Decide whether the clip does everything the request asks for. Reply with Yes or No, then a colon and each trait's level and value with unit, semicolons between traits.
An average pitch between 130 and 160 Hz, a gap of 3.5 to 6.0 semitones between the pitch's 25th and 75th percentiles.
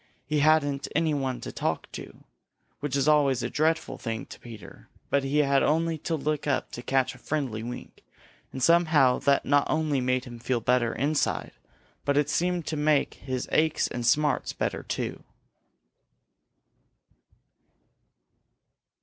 No: medium, 140 Hz; average, 3.1 semitones